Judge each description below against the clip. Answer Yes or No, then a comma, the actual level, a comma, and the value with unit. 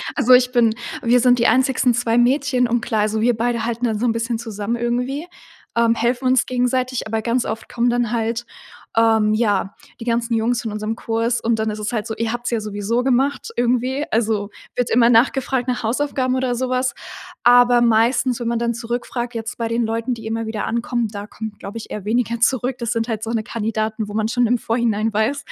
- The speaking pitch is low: No, high, 235 Hz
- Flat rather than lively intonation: Yes, narrow, 1.7 semitones